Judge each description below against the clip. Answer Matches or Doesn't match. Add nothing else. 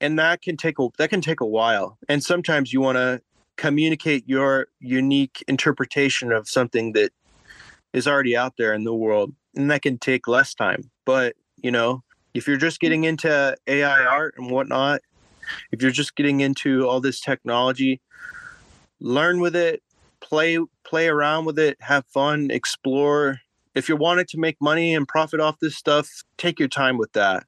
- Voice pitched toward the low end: Doesn't match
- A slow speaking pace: Doesn't match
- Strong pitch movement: Doesn't match